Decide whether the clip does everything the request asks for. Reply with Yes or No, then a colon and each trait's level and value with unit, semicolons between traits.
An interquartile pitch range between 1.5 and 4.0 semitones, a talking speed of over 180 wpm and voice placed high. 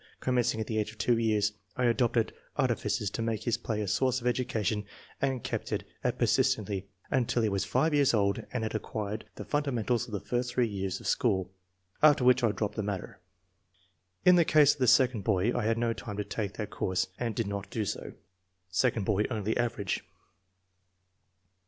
No: average, 3.0 semitones; average, 195 wpm; low, 115 Hz